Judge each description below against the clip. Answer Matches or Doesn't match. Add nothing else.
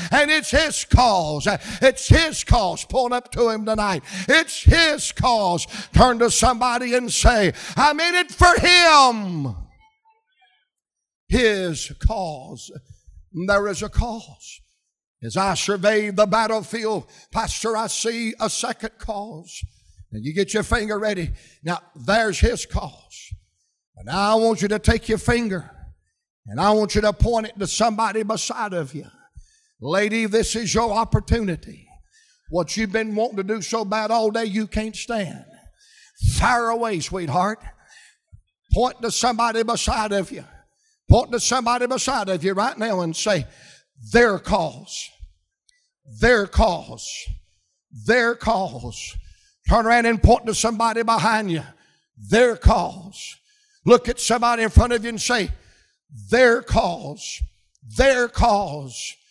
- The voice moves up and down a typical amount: Matches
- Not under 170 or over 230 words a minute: Doesn't match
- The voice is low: Doesn't match